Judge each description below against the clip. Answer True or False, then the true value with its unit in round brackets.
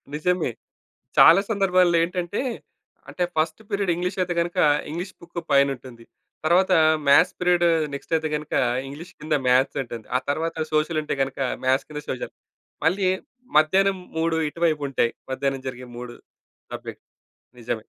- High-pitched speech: False (160 Hz)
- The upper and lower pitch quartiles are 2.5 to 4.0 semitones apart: False (4.5 semitones)